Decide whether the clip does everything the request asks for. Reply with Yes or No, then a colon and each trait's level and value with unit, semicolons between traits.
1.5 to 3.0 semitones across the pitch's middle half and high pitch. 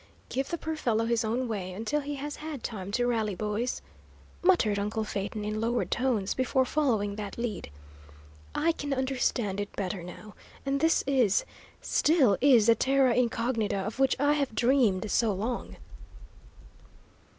No: average, 4.4 semitones; high, 235 Hz